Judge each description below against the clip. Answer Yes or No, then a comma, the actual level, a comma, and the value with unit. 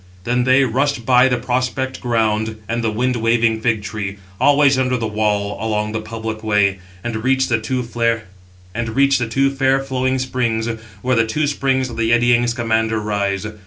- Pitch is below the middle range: Yes, low, 115 Hz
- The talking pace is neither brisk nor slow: Yes, average, 160 wpm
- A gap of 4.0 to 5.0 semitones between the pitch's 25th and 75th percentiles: No, average, 2.8 semitones